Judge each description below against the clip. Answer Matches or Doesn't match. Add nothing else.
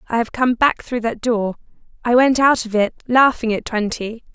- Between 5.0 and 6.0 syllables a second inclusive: Doesn't match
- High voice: Matches